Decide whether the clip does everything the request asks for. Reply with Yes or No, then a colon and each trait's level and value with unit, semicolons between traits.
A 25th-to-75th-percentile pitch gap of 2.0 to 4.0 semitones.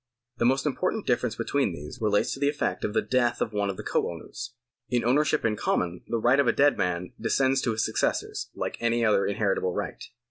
No: average, 4.6 semitones